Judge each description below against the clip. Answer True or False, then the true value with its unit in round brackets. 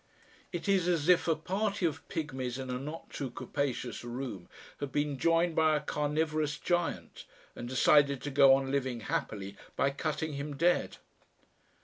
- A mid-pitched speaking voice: True (145 Hz)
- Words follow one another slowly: False (160 wpm)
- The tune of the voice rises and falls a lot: False (3.2 semitones)